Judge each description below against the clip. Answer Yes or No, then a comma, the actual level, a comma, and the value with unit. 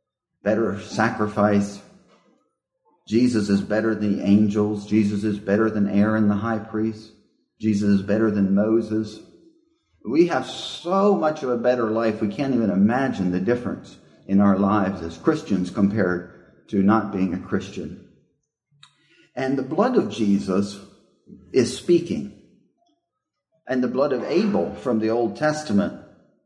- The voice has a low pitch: Yes, low, 110 Hz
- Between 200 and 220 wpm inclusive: No, average, 140 wpm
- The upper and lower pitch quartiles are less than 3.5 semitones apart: No, average, 3.8 semitones